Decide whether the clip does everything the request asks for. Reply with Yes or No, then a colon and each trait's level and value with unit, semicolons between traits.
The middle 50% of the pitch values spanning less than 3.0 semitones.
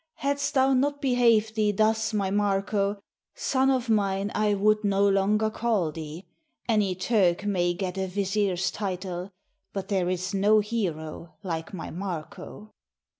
Yes: narrow, 2.6 semitones